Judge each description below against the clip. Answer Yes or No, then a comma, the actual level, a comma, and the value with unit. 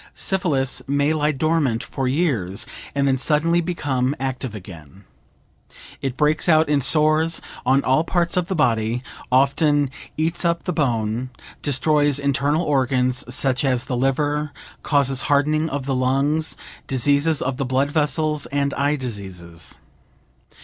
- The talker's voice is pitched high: No, medium, 140 Hz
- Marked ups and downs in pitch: No, average, 3.1 semitones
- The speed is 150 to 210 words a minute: No, average, 140 wpm